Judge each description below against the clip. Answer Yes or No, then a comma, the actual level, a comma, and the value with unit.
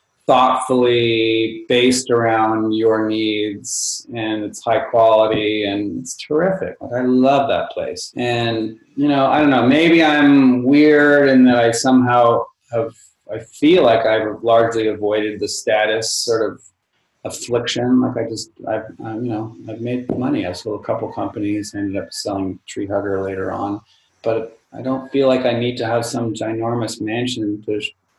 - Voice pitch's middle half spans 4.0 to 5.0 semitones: No, narrow, 2.5 semitones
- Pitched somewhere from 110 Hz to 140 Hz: Yes, low, 115 Hz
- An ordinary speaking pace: Yes, average, 170 wpm